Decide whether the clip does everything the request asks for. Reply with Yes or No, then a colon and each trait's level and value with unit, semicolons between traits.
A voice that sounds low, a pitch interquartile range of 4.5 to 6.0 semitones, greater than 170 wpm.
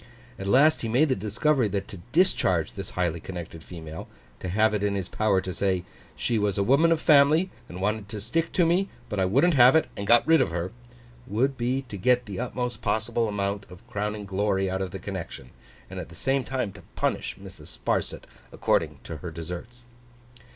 Yes: low, 105 Hz; average, 4.9 semitones; average, 200 wpm